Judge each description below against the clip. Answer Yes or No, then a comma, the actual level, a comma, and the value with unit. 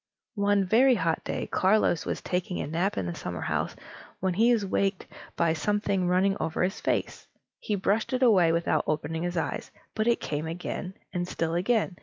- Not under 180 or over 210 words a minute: Yes, average, 185 wpm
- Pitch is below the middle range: No, medium, 185 Hz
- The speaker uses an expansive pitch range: No, average, 3.6 semitones